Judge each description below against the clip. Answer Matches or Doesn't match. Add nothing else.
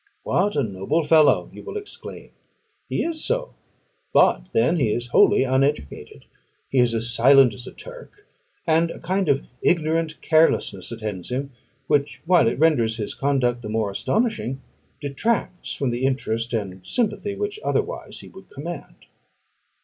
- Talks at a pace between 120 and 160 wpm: Matches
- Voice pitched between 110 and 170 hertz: Matches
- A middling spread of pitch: Doesn't match